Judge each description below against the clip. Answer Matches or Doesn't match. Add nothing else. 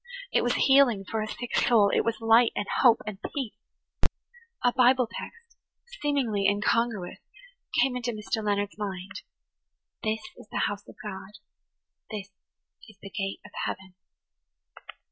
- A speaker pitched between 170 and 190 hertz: Doesn't match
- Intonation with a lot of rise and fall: Doesn't match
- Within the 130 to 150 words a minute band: Matches